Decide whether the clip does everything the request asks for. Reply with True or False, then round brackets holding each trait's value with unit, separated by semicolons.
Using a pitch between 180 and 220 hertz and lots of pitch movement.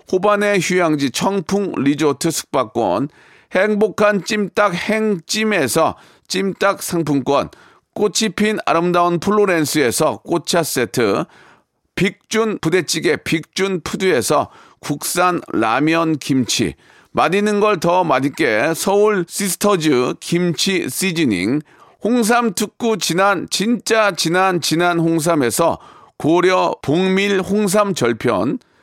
False (185 Hz; 3.9 semitones)